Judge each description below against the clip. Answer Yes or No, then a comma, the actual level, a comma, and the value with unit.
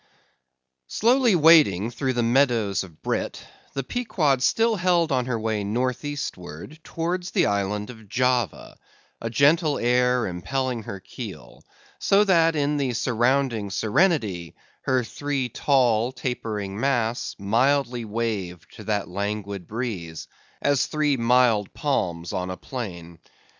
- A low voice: Yes, low, 120 Hz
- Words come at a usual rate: No, slow, 130 wpm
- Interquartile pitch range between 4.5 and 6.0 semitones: Yes, wide, 5.5 semitones